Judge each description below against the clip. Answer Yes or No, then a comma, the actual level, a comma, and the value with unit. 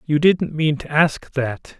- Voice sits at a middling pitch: Yes, medium, 150 Hz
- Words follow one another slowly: No, average, 200 wpm